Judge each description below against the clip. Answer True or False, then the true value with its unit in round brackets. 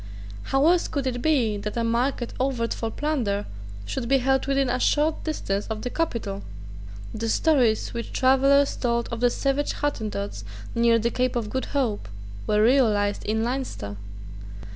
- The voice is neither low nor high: False (245 Hz)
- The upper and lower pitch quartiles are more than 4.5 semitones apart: False (3.7 semitones)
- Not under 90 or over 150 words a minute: False (165 wpm)